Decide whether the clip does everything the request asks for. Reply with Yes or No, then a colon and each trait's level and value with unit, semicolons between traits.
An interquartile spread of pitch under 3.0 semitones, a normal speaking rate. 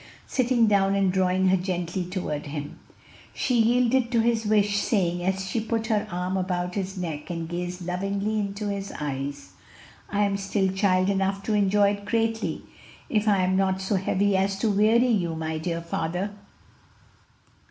Yes: narrow, 2.5 semitones; average, 170 wpm